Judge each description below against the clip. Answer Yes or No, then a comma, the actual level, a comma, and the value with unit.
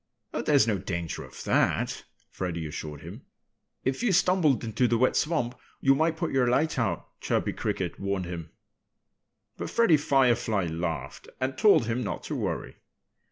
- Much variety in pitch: Yes, wide, 8.0 semitones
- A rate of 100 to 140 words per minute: No, average, 160 wpm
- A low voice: Yes, low, 120 Hz